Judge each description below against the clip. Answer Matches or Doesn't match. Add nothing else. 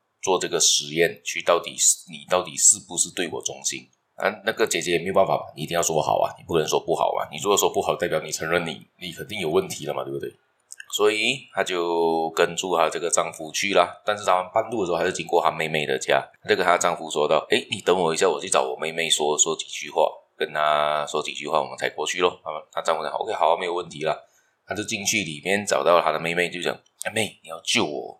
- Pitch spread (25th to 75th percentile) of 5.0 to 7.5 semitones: Doesn't match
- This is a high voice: Doesn't match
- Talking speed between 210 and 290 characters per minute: Doesn't match